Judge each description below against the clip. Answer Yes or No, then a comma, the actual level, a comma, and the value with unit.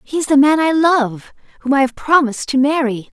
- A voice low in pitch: No, very high, 275 Hz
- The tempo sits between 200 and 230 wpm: Yes, fast, 205 wpm